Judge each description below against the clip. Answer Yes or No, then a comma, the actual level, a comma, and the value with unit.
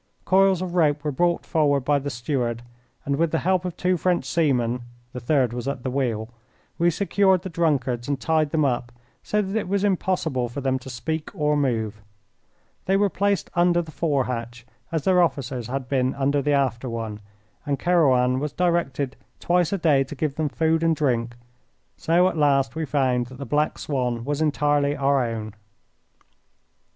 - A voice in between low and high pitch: Yes, medium, 145 Hz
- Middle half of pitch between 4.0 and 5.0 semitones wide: Yes, average, 4.7 semitones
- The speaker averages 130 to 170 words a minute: No, average, 185 wpm